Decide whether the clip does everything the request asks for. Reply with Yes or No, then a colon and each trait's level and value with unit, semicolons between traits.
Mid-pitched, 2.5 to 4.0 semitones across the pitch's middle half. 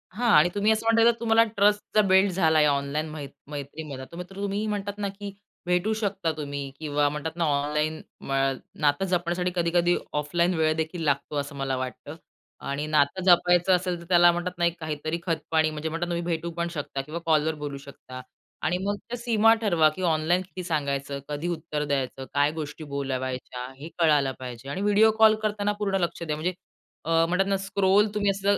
No: medium, 165 Hz; average, 4.6 semitones